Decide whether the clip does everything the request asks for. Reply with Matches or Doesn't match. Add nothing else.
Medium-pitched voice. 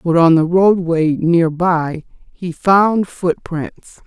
Matches